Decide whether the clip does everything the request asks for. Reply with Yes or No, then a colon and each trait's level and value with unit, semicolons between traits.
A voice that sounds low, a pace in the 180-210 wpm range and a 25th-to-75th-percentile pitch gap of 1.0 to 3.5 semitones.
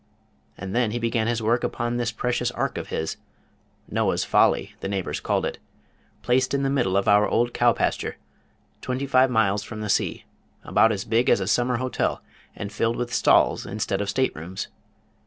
Yes: low, 115 Hz; average, 190 wpm; average, 3.2 semitones